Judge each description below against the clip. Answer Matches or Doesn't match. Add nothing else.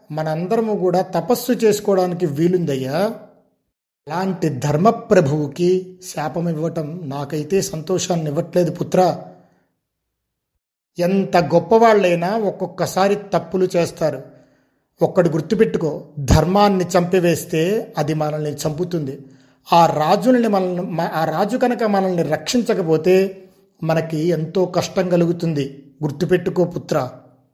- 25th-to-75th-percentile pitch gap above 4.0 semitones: Doesn't match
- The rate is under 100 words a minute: Matches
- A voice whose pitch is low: Doesn't match